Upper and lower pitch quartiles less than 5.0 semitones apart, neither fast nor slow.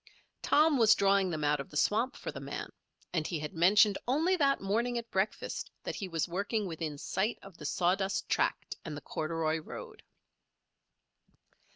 No: wide, 5.5 semitones; average, 175 wpm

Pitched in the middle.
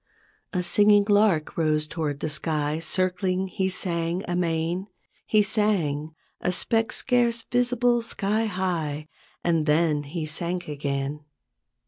Yes: medium, 175 Hz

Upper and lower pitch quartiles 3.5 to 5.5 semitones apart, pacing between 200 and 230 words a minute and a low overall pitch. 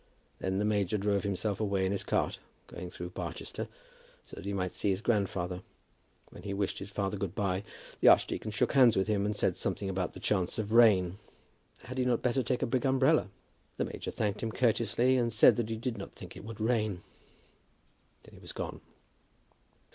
No: average, 3.1 semitones; fast, 205 wpm; low, 105 Hz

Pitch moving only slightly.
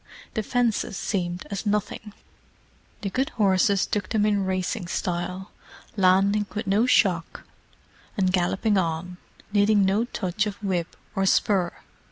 Yes: narrow, 2.2 semitones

